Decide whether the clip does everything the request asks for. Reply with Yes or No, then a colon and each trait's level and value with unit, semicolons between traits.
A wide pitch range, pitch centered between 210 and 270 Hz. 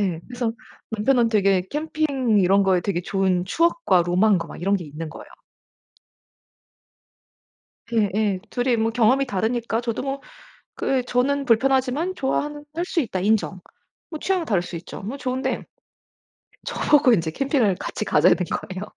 Yes: wide, 5.9 semitones; high, 225 Hz